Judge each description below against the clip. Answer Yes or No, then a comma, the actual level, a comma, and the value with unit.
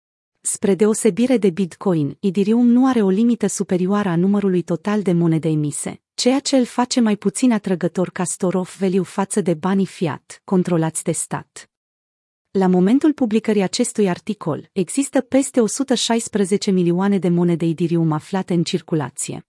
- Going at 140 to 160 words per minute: Yes, average, 145 wpm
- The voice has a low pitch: No, high, 195 Hz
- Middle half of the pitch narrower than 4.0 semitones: No, average, 4.3 semitones